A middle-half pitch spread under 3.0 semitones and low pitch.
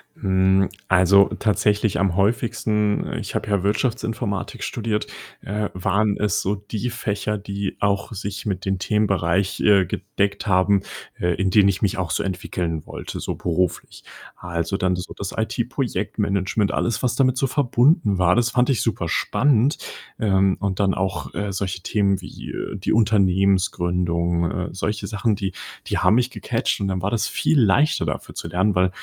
Yes: narrow, 2.5 semitones; low, 100 Hz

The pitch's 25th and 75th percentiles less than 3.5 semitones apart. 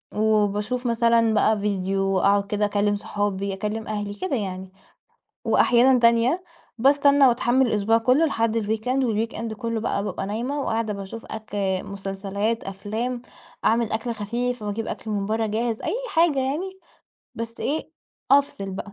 Yes: average, 2.9 semitones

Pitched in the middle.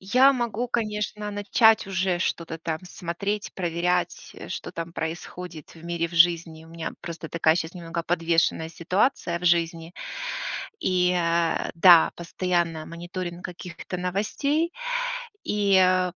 Yes: medium, 175 Hz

